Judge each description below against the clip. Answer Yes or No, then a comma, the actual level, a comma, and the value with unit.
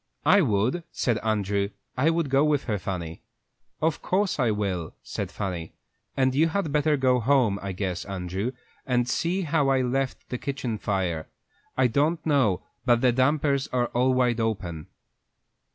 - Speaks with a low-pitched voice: Yes, low, 125 Hz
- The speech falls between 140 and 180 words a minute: Yes, average, 165 wpm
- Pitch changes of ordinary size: No, wide, 6.0 semitones